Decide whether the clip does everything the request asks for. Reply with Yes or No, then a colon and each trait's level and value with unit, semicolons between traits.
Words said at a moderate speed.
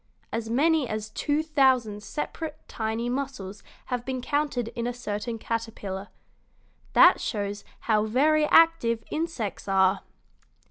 No: slow, 125 wpm